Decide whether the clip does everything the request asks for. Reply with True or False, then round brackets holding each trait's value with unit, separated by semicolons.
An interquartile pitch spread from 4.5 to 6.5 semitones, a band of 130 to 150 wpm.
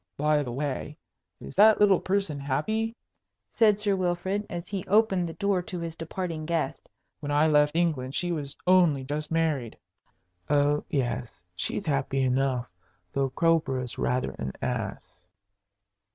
True (4.9 semitones; 145 wpm)